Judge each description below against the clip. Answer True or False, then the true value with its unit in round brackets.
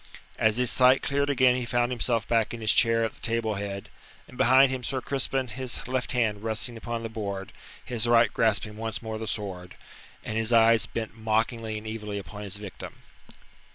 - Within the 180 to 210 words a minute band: True (195 wpm)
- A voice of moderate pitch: False (115 Hz)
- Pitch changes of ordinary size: False (2.1 semitones)